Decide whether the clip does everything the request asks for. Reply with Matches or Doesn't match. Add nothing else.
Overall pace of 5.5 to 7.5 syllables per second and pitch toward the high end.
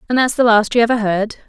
Matches